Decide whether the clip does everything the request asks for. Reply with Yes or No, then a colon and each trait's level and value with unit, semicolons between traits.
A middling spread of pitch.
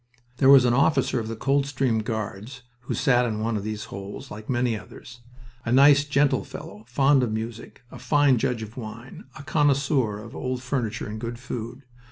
Yes: average, 3.6 semitones